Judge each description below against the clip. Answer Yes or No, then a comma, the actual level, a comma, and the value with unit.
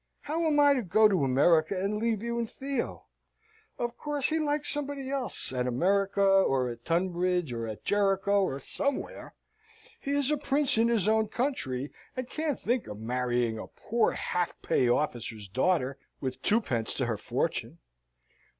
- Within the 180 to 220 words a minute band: No, average, 170 wpm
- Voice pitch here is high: Yes, high, 195 Hz